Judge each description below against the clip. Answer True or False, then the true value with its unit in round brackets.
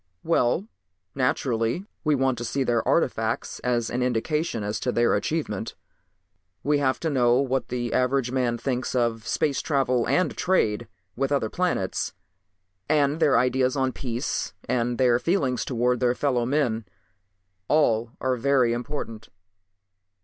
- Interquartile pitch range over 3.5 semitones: False (2.8 semitones)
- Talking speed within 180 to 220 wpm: False (140 wpm)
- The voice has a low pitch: True (125 Hz)